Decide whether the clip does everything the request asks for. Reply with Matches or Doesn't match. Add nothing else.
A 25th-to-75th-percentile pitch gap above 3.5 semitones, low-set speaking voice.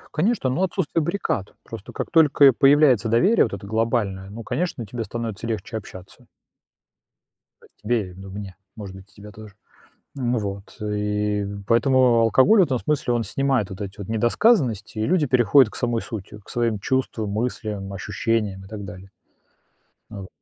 Matches